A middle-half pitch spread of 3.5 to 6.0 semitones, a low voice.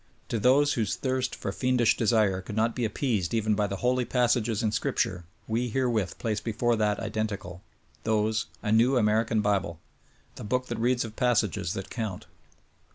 No: average, 2.7 semitones; low, 110 Hz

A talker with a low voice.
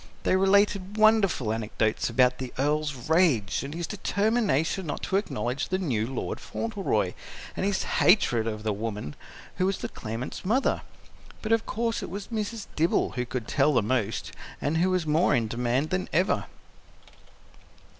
No: medium, 155 Hz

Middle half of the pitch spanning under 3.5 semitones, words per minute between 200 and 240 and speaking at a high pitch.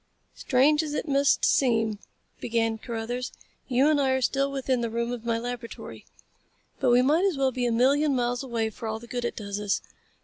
Yes: average, 2.9 semitones; fast, 205 wpm; high, 245 Hz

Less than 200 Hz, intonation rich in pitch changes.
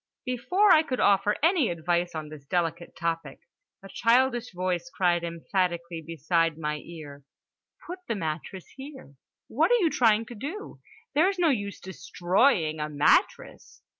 Yes: medium, 185 Hz; wide, 7.6 semitones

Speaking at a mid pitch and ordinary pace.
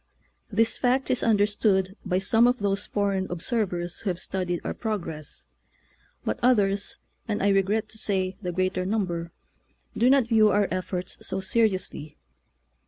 No: high, 195 Hz; average, 155 wpm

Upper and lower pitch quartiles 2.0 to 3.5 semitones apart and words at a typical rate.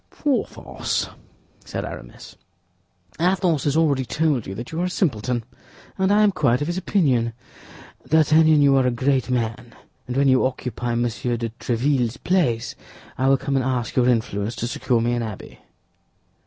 No: average, 4.7 semitones; average, 170 wpm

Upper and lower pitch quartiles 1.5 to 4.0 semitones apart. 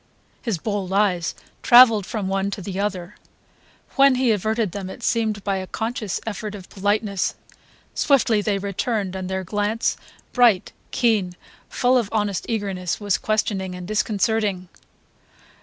Yes: average, 2.7 semitones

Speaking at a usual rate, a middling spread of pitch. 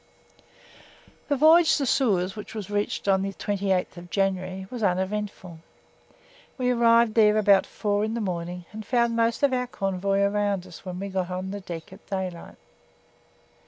Yes: average, 160 wpm; average, 3.2 semitones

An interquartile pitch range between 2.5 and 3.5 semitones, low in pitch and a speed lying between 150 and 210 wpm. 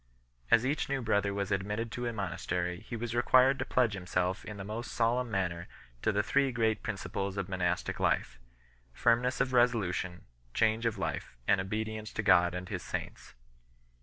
No: average, 4.0 semitones; low, 105 Hz; average, 180 wpm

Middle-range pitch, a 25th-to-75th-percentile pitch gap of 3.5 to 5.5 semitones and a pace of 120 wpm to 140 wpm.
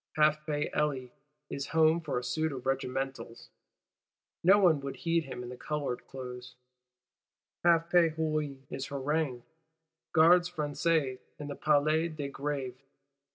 No: medium, 150 Hz; average, 3.1 semitones; slow, 135 wpm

